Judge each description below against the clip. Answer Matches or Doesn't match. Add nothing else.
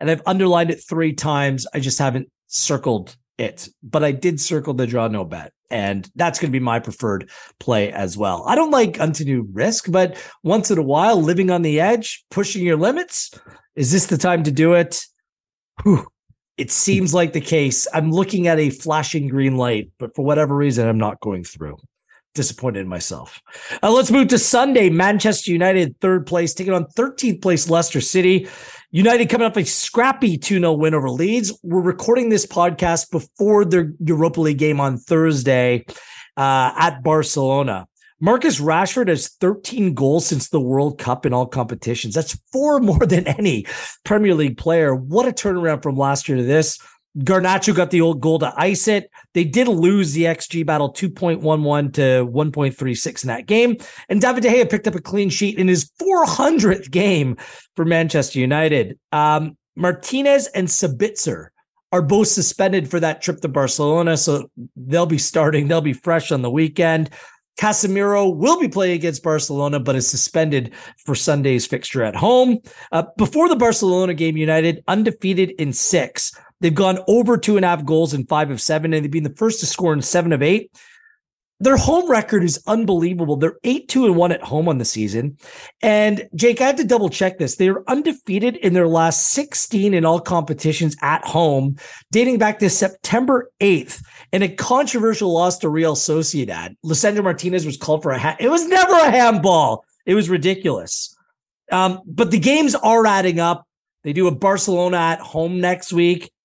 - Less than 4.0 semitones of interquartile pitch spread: Doesn't match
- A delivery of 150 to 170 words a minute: Doesn't match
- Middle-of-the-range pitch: Matches